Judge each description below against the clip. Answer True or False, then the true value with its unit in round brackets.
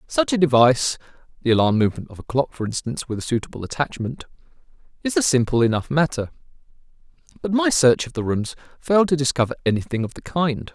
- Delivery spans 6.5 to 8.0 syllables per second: True (6.6 syllables/s)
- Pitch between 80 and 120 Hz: False (135 Hz)